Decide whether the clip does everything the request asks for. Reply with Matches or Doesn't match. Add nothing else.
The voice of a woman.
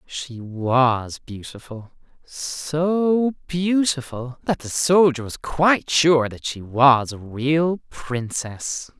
Doesn't match